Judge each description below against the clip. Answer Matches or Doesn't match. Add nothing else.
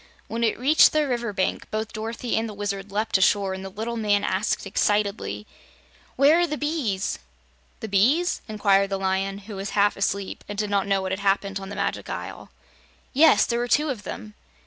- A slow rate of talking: Doesn't match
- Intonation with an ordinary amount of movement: Matches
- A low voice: Doesn't match